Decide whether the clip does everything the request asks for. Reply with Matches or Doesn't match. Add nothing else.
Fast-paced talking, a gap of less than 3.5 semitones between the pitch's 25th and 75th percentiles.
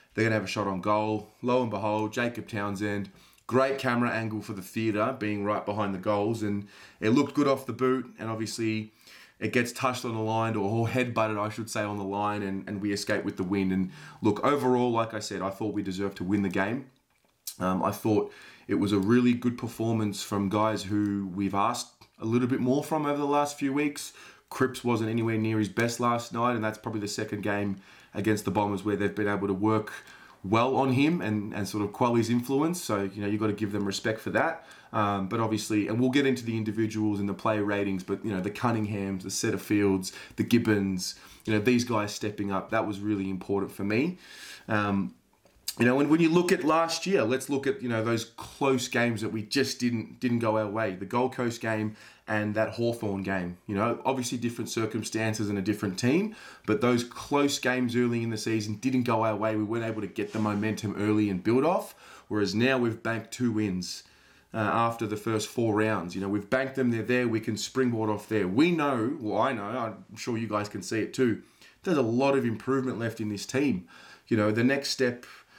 Matches